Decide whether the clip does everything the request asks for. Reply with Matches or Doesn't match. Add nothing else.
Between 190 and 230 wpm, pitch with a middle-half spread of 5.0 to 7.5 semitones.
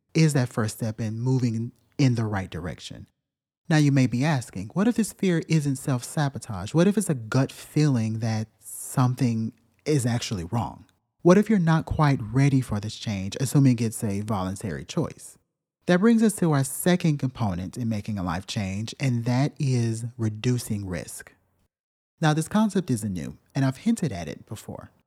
Doesn't match